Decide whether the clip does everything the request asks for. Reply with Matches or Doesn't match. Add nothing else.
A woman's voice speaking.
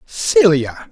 Doesn't match